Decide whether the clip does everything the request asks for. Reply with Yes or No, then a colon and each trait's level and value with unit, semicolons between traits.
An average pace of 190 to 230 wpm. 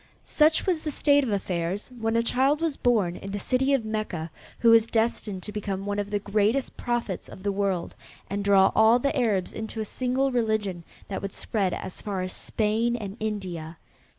Yes: average, 200 wpm